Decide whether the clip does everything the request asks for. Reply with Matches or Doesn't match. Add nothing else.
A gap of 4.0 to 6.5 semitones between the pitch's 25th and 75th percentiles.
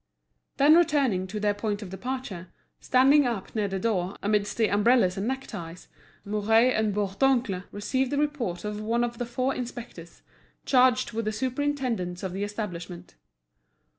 Matches